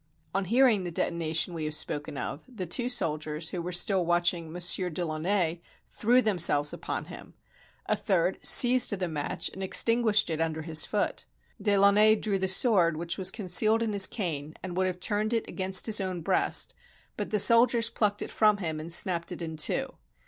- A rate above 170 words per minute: Yes, average, 190 wpm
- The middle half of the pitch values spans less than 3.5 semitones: No, average, 4.2 semitones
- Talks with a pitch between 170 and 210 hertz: Yes, medium, 185 Hz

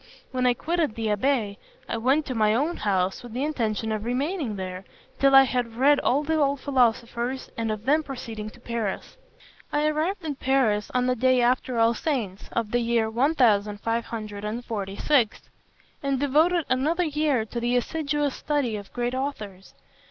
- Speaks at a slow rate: No, average, 165 wpm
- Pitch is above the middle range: Yes, high, 245 Hz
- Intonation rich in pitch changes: No, average, 4.3 semitones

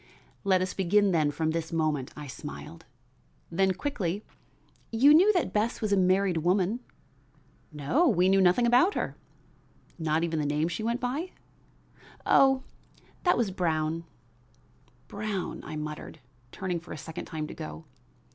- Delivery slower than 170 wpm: Yes, average, 150 wpm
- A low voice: No, medium, 185 Hz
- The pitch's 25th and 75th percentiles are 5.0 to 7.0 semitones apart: Yes, average, 5.3 semitones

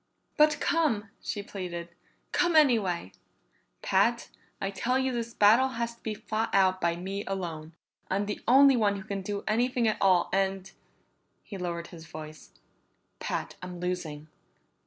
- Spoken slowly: No, average, 155 wpm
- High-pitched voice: Yes, high, 200 Hz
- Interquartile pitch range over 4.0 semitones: Yes, average, 4.6 semitones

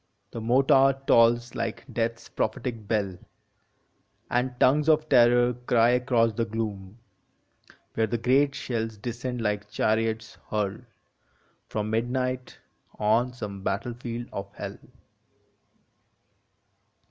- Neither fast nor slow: No, slow, 110 wpm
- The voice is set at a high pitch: No, low, 115 Hz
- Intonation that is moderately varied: No, narrow, 2.2 semitones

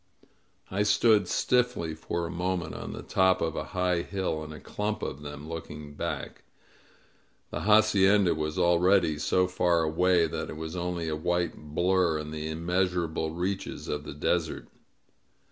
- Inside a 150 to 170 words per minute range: Yes, average, 160 wpm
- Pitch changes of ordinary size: Yes, average, 3.0 semitones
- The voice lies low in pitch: Yes, very low, 85 Hz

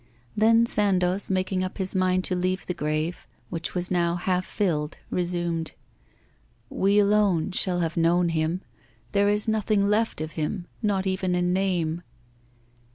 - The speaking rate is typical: Yes, average, 150 wpm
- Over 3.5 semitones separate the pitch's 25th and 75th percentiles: No, narrow, 2.5 semitones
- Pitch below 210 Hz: Yes, medium, 185 Hz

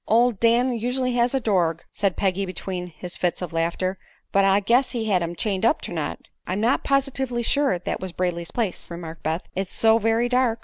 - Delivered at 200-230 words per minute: Yes, fast, 205 wpm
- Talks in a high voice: Yes, high, 205 Hz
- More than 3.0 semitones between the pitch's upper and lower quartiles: Yes, average, 5.0 semitones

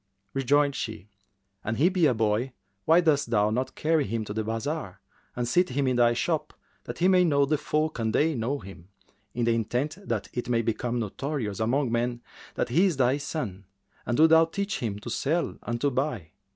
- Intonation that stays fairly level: No, average, 5.0 semitones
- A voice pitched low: Yes, low, 125 Hz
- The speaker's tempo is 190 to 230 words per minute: Yes, fast, 205 wpm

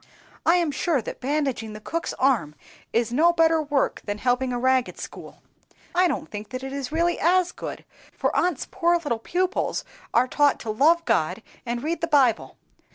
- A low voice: No, very high, 280 Hz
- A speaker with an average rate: Yes, average, 185 wpm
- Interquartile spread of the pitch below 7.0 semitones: Yes, average, 5.3 semitones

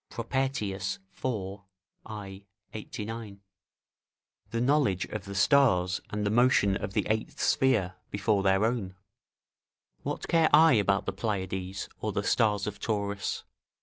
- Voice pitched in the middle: No, low, 105 Hz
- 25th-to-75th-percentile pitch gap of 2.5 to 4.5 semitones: Yes, average, 3.1 semitones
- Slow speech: Yes, slow, 130 wpm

